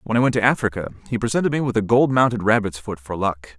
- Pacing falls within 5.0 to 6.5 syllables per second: No, 6.7 syllables/s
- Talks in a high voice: No, low, 110 Hz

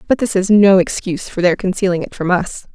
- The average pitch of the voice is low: No, high, 190 Hz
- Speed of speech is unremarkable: No, fast, 240 wpm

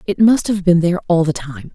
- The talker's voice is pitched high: No, medium, 175 Hz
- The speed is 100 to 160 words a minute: No, fast, 275 wpm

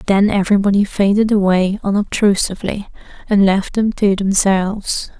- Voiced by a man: No, female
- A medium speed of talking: No, slow, 115 wpm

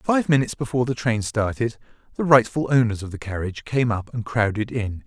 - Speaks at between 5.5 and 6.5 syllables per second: Yes, 5.8 syllables/s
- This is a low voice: Yes, low, 115 Hz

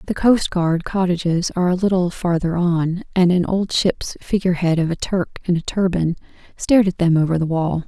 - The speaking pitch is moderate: Yes, medium, 175 Hz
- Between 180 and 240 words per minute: Yes, average, 190 wpm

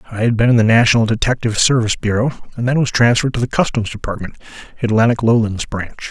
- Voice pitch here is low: Yes, low, 115 Hz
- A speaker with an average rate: Yes, average, 195 wpm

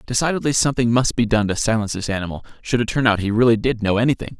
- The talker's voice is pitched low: Yes, low, 115 Hz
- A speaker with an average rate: No, fast, 245 wpm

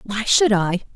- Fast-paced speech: No, average, 190 wpm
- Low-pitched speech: No, high, 215 Hz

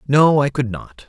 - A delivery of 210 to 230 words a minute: Yes, fast, 220 wpm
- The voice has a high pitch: No, low, 130 Hz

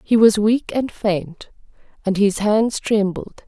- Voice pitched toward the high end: Yes, high, 210 Hz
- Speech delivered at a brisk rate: No, average, 155 wpm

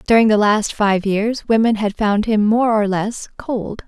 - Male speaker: No, female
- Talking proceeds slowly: No, average, 200 wpm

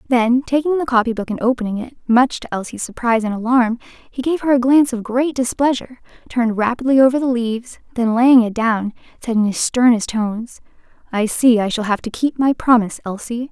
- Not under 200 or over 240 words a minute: Yes, fast, 205 wpm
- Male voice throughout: No, female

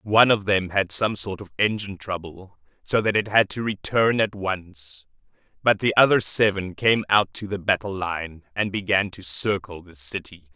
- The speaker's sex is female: No, male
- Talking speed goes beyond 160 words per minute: Yes, average, 190 wpm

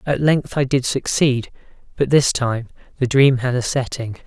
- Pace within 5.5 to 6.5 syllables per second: No, 4.5 syllables/s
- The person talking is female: No, male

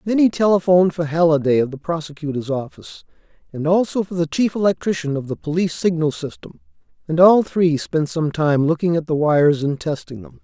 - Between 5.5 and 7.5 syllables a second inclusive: Yes, 5.8 syllables/s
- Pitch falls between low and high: Yes, medium, 165 Hz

